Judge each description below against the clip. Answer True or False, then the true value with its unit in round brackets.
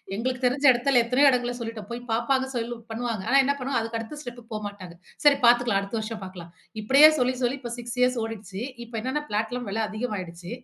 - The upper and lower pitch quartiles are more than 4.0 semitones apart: False (2.8 semitones)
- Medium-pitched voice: False (235 Hz)